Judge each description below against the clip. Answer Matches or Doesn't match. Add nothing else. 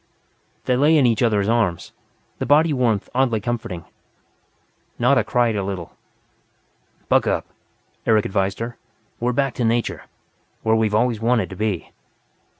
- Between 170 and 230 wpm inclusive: Doesn't match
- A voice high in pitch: Doesn't match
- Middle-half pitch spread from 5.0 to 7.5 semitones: Doesn't match